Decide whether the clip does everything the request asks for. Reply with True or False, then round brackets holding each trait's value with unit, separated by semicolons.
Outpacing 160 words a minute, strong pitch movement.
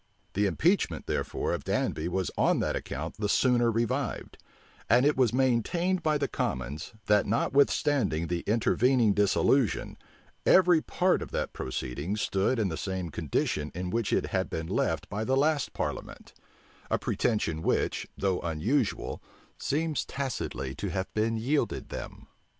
False (150 wpm; 6.9 semitones)